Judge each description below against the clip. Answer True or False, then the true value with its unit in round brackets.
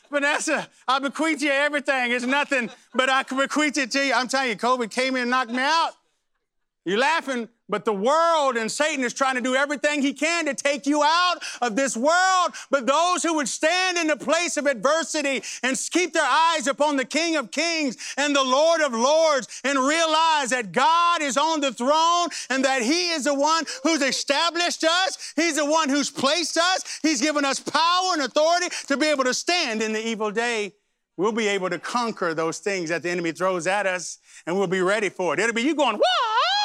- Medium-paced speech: False (215 wpm)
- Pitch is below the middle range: False (285 Hz)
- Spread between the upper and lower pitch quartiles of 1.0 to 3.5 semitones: False (4.1 semitones)